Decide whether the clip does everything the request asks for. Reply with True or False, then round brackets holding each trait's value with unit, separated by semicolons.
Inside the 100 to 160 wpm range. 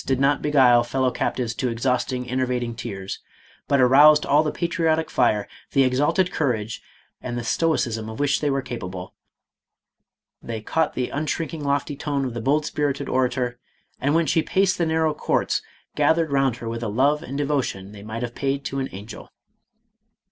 False (175 wpm)